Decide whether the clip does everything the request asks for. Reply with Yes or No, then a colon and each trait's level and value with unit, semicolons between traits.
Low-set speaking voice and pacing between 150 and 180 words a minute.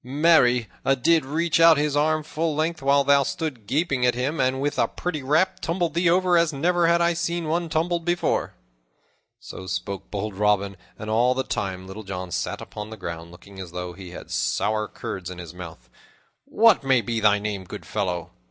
No: low, 130 Hz; average, 200 wpm